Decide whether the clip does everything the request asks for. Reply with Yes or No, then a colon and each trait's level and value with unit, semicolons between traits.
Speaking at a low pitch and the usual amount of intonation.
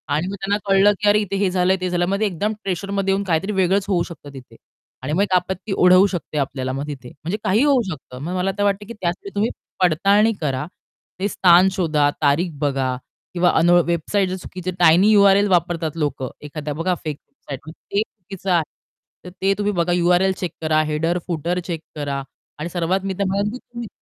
No: medium, 180 Hz; average, 3.8 semitones